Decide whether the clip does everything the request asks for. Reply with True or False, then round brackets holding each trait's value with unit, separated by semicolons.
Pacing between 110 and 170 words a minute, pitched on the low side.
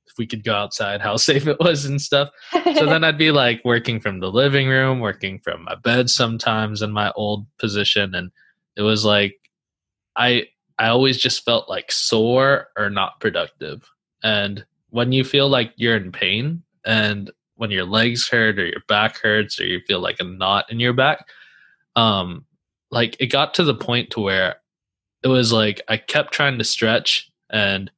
False (190 wpm; 115 Hz)